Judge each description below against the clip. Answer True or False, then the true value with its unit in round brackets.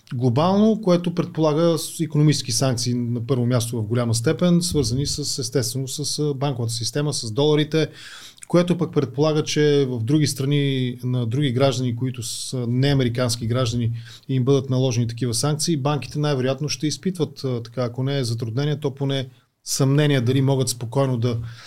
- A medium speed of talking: True (150 wpm)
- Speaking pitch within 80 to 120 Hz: False (135 Hz)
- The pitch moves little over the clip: False (3.2 semitones)